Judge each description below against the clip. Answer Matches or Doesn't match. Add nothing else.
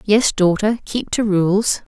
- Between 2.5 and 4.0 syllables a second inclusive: Matches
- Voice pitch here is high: Matches